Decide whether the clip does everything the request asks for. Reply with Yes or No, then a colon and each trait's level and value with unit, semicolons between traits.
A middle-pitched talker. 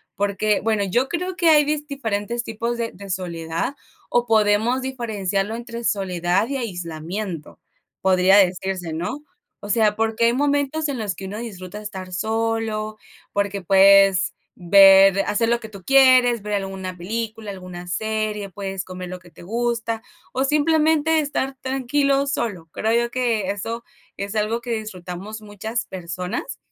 No: high, 215 Hz